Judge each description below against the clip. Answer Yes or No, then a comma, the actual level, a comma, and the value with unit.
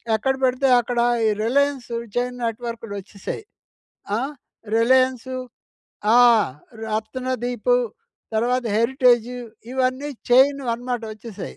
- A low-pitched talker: No, high, 245 Hz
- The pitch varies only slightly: Yes, narrow, 2.1 semitones